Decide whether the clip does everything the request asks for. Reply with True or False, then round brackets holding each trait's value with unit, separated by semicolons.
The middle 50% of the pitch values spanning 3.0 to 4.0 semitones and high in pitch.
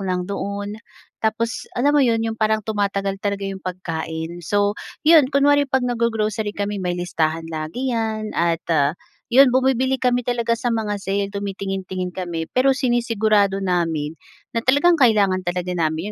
False (4.7 semitones; 205 Hz)